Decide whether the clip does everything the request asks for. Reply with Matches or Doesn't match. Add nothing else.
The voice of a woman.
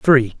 Doesn't match